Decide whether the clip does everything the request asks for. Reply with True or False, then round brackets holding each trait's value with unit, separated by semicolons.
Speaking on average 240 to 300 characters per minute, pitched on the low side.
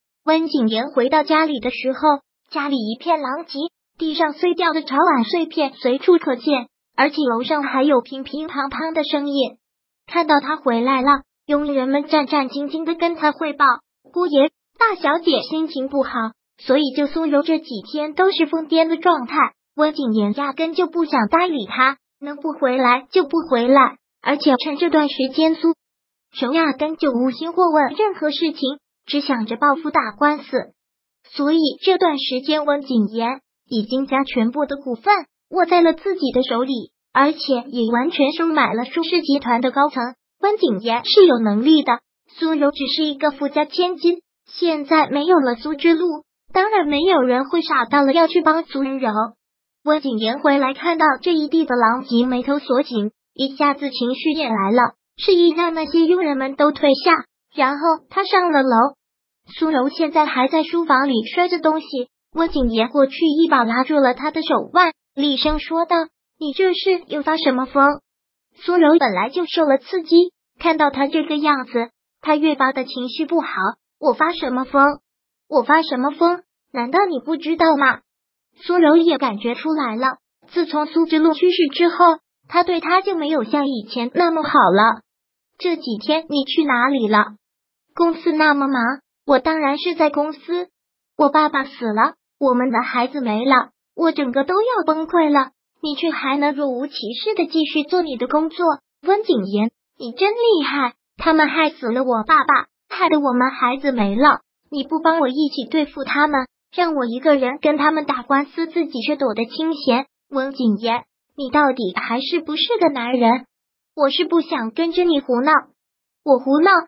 False (255 characters per minute; 295 Hz)